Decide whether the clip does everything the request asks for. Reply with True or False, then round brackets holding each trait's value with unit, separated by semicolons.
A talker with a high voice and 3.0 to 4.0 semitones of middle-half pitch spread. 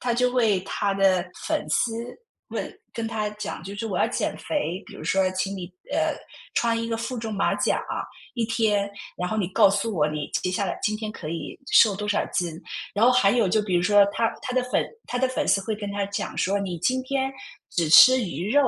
True (210 Hz; 3.4 semitones)